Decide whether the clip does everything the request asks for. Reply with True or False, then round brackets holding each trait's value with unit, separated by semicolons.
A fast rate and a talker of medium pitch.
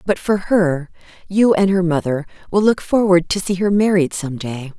False (190 wpm; 180 Hz)